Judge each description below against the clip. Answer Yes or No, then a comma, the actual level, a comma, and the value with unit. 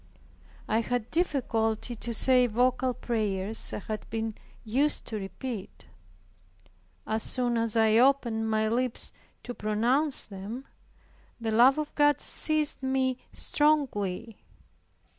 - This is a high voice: Yes, high, 235 Hz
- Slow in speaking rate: Yes, slow, 120 wpm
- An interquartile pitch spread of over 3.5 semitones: No, average, 3.2 semitones